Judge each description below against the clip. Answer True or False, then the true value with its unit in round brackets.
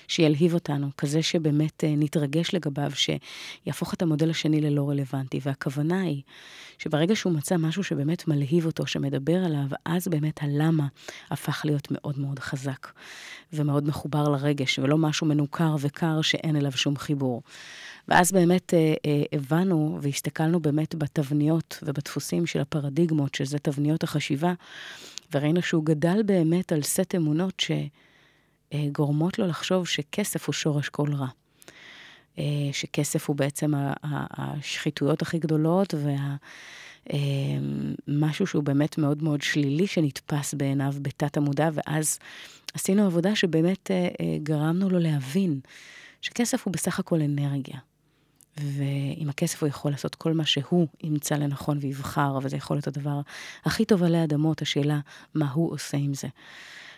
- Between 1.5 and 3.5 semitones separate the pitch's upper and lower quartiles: True (2.4 semitones)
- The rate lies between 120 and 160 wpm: True (135 wpm)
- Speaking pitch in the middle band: True (150 Hz)